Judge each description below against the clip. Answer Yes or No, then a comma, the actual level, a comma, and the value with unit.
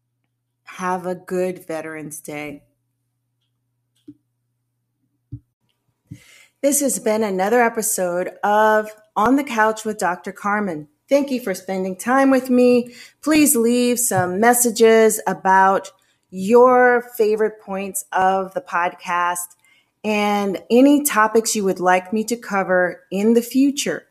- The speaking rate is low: Yes, slow, 115 wpm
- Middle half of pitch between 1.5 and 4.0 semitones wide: No, average, 5.2 semitones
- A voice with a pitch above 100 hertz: Yes, high, 190 Hz